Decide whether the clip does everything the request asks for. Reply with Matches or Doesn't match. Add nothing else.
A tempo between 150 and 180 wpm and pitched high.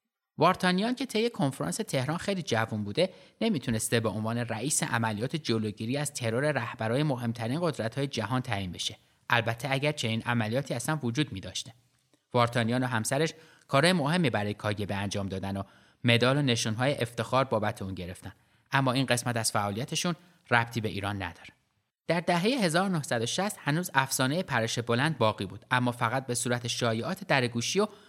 Doesn't match